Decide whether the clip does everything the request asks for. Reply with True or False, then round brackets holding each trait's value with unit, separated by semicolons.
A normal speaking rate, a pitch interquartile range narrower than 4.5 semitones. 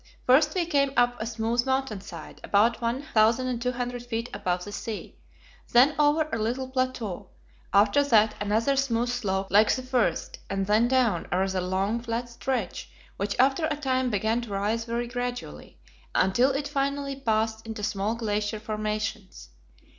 True (155 wpm; 3.6 semitones)